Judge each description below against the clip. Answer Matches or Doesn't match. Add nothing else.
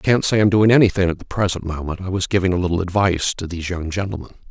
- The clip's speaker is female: Doesn't match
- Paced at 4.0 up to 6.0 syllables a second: Doesn't match